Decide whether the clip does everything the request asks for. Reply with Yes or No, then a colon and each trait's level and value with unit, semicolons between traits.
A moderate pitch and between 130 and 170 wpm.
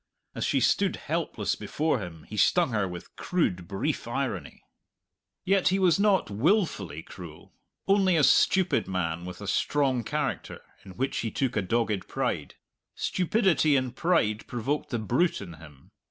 No: low, 120 Hz; average, 155 wpm